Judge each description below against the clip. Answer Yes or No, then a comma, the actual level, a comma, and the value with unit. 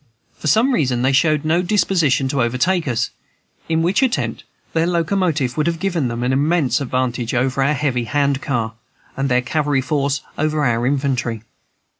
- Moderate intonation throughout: Yes, average, 4.2 semitones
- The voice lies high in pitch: No, medium, 140 Hz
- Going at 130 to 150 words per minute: No, average, 170 wpm